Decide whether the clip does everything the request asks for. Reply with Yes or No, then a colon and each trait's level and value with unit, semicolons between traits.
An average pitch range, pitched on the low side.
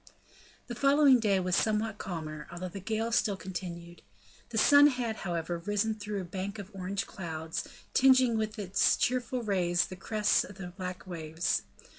No: average, 4.0 semitones; high, 195 Hz